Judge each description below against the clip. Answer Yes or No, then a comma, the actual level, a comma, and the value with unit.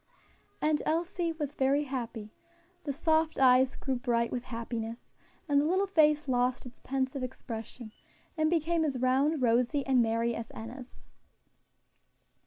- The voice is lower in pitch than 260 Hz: No, very high, 265 Hz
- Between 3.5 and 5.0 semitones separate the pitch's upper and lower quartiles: Yes, average, 4.0 semitones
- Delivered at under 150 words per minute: Yes, average, 140 wpm